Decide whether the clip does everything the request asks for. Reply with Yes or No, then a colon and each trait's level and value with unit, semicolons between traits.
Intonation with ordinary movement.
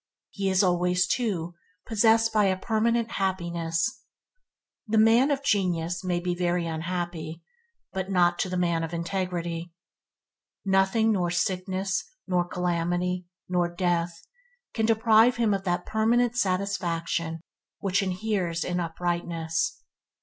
Yes: average, 3.5 semitones